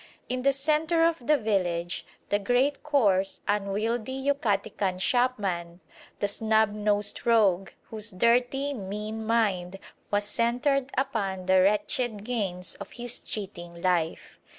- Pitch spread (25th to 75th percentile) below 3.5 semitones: No, average, 4.4 semitones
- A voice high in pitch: Yes, high, 215 Hz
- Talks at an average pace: No, slow, 120 wpm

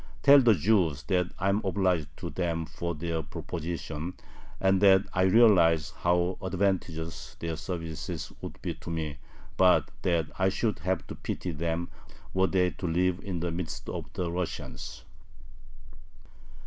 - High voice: No, very low, 90 Hz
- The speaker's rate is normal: Yes, average, 150 wpm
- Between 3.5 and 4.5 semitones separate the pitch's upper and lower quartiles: No, narrow, 2.4 semitones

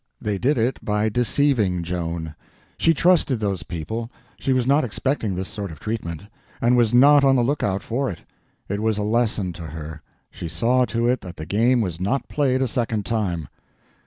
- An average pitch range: No, wide, 5.7 semitones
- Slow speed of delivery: No, average, 190 wpm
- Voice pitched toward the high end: No, low, 110 Hz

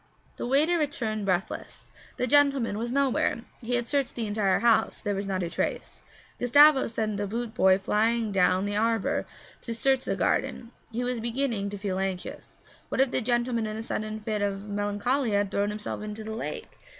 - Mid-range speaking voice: No, high, 220 Hz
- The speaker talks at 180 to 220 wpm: Yes, average, 190 wpm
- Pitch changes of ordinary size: Yes, average, 3.2 semitones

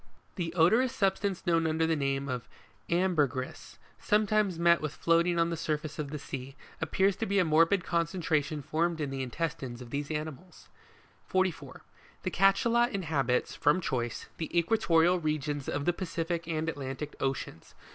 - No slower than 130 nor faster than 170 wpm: Yes, average, 155 wpm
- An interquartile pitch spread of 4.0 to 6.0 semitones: No, average, 3.6 semitones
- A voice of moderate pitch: Yes, medium, 165 Hz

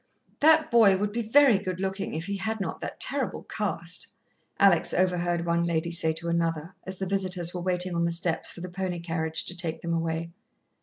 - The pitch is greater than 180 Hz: No, medium, 175 Hz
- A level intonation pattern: Yes, narrow, 2.3 semitones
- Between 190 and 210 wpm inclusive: Yes, fast, 205 wpm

